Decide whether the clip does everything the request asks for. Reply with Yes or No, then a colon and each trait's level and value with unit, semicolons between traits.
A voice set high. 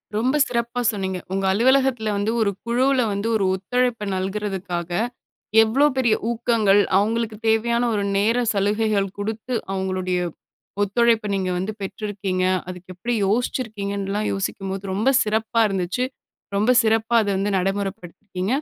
Yes: high, 210 Hz